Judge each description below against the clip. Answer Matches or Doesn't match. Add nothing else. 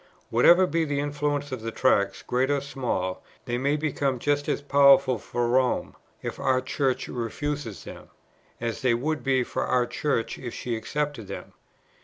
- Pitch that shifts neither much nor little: Matches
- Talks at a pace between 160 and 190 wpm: Matches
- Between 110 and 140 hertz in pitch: Matches